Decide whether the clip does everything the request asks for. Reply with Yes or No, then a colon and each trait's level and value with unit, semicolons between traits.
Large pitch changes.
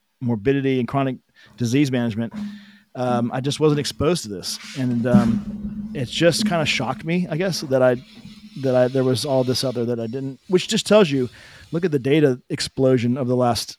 Yes: wide, 6.3 semitones